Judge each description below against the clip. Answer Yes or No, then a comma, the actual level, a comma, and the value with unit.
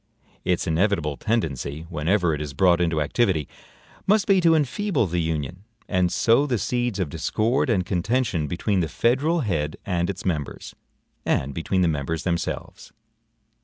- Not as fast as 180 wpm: Yes, average, 155 wpm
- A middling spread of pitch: No, wide, 6.4 semitones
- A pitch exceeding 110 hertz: No, very low, 90 Hz